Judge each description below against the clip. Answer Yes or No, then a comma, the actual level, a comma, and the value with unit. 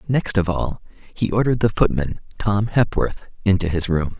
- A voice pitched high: No, low, 100 Hz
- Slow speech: No, average, 170 wpm